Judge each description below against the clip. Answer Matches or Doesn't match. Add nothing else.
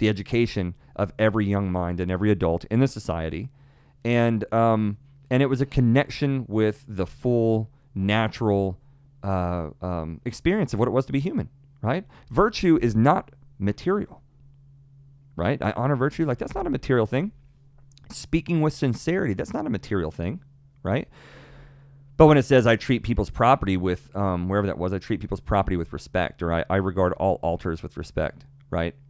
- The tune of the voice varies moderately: Doesn't match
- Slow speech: Doesn't match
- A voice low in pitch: Matches